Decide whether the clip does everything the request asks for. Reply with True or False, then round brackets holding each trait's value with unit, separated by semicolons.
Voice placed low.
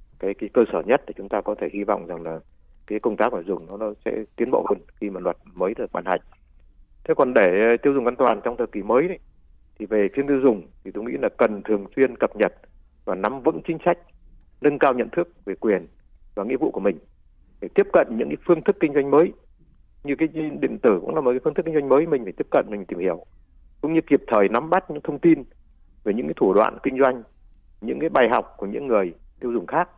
True (125 Hz)